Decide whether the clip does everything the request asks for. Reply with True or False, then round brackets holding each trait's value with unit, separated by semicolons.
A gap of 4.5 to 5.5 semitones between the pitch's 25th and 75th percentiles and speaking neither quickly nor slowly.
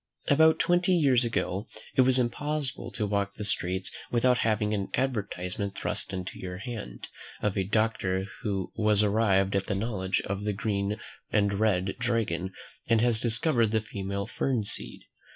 False (3.4 semitones; 160 wpm)